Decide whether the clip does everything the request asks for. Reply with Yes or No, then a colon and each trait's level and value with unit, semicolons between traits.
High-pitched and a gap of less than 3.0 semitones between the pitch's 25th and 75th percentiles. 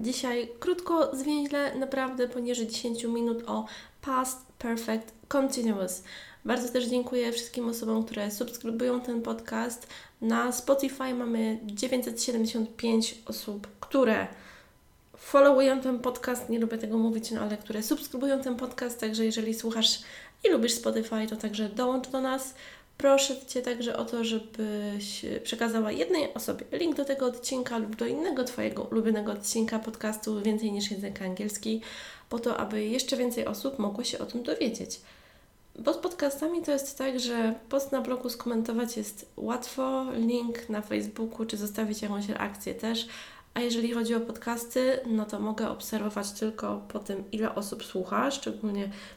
Yes: high, 235 Hz; narrow, 2.6 semitones